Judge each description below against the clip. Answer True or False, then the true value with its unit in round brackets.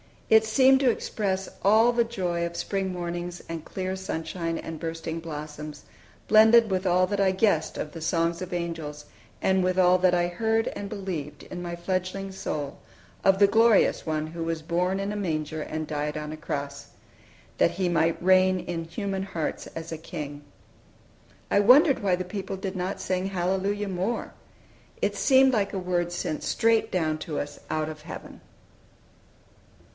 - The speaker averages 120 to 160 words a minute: False (175 wpm)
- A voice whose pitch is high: False (180 Hz)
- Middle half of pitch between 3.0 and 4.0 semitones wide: True (3.3 semitones)